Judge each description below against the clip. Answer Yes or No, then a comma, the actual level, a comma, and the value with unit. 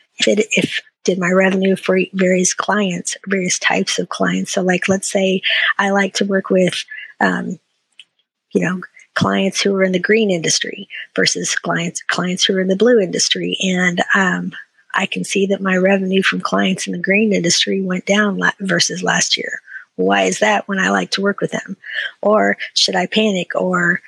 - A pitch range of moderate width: No, narrow, 1.4 semitones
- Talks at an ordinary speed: Yes, average, 190 wpm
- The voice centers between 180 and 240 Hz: Yes, high, 190 Hz